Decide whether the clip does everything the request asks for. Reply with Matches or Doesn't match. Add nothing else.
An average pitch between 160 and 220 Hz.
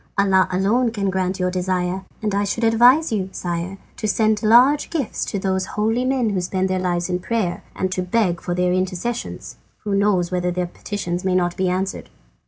Matches